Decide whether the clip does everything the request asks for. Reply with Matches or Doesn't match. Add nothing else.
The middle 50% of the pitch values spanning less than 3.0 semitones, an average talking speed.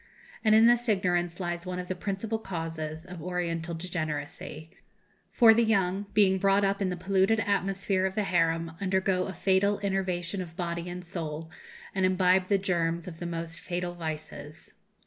Matches